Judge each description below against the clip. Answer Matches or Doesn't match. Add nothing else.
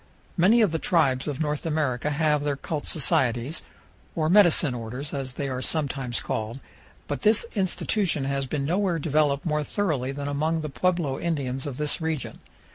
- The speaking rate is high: Doesn't match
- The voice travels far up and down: Doesn't match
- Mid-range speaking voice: Matches